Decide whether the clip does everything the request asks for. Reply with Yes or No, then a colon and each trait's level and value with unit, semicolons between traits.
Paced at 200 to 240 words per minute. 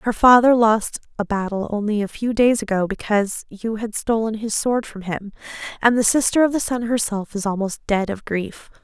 Yes: fast, 205 wpm